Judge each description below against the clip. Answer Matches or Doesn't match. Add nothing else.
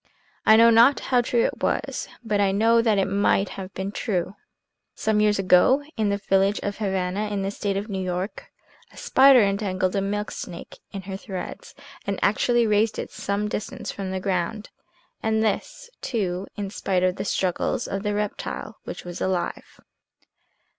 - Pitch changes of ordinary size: Doesn't match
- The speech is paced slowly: Doesn't match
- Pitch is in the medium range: Doesn't match